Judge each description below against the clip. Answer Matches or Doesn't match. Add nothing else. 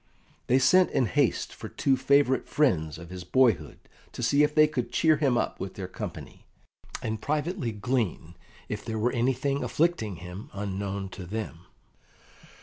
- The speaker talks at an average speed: Matches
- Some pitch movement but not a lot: Doesn't match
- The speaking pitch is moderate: Doesn't match